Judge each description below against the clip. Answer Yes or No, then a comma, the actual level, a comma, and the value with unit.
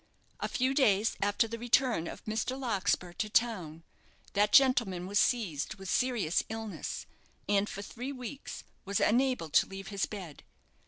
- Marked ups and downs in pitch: No, average, 4.1 semitones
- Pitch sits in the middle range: No, high, 210 Hz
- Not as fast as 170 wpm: Yes, average, 155 wpm